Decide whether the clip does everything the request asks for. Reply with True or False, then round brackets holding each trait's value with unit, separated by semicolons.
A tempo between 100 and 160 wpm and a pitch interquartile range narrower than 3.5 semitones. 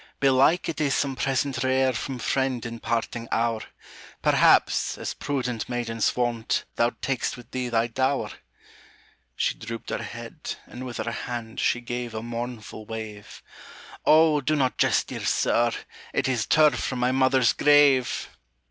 True (155 wpm; 2.4 semitones)